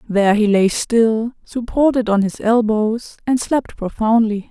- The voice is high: Yes, high, 225 Hz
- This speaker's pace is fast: No, average, 145 wpm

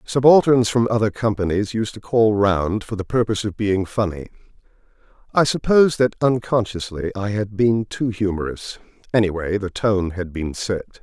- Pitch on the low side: Yes, low, 105 Hz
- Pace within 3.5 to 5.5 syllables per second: Yes, 5.0 syllables/s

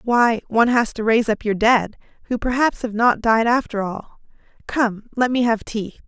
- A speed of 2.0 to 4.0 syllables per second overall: No, 4.8 syllables/s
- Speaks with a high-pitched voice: Yes, high, 225 Hz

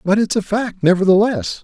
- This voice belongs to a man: Yes, male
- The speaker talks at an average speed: Yes, average, 185 wpm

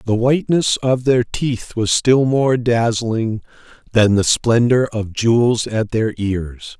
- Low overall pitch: Yes, low, 115 Hz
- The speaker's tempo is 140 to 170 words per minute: Yes, average, 150 wpm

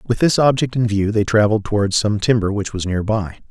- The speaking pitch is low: Yes, low, 110 Hz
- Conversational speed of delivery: No, fast, 240 wpm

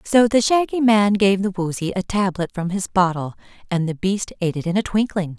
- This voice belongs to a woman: Yes, female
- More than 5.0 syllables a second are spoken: Yes, 5.4 syllables/s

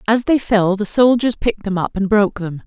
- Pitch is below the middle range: No, high, 210 Hz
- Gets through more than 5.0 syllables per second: Yes, 5.6 syllables/s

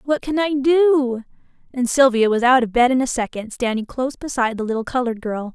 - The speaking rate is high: Yes, fast, 215 wpm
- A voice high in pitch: Yes, very high, 250 Hz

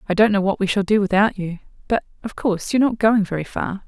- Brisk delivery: Yes, fast, 265 wpm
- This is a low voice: No, high, 200 Hz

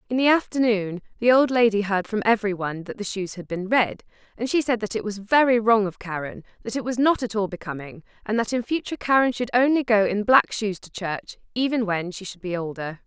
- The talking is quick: Yes, fast, 235 wpm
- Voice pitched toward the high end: Yes, high, 215 Hz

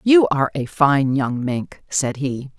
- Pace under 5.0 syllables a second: Yes, 3.9 syllables/s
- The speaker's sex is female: Yes, female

